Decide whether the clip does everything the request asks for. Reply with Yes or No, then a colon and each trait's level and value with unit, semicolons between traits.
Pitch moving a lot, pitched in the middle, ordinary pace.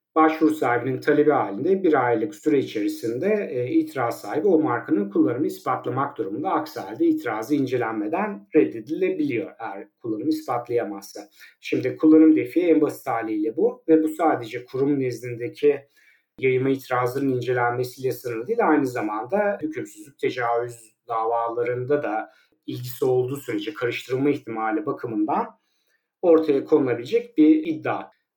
Yes: wide, 8.3 semitones; medium, 150 Hz; average, 120 wpm